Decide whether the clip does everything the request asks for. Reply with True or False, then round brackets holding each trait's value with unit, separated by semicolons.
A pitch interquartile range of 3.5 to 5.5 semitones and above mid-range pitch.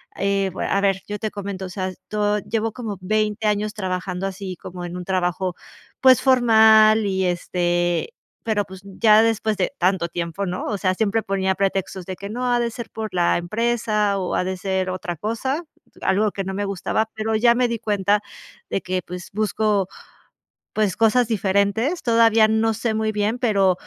False (2.8 semitones; 205 Hz)